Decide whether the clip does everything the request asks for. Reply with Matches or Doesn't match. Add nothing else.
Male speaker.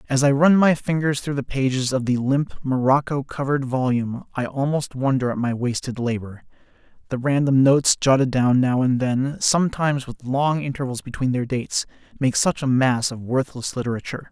Matches